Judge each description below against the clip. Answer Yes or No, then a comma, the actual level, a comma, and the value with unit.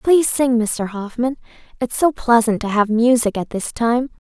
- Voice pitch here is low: No, high, 240 Hz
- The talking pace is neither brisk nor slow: Yes, average, 185 wpm